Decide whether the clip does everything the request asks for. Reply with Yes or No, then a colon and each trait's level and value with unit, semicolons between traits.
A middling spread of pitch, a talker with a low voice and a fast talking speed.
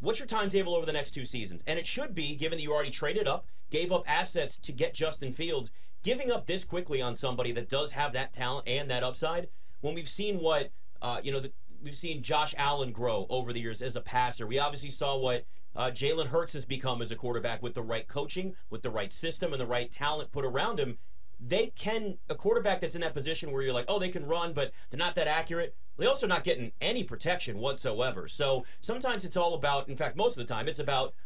No: average, 5.0 semitones; medium, 145 Hz; fast, 240 wpm